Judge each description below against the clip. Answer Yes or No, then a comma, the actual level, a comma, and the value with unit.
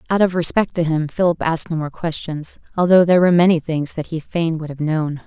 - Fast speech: Yes, fast, 240 wpm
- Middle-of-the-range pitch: Yes, medium, 165 Hz